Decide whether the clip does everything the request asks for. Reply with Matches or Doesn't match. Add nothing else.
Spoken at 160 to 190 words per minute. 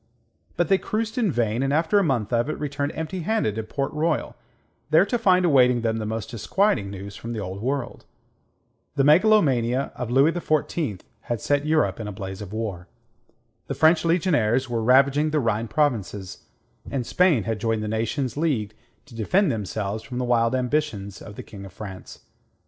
Matches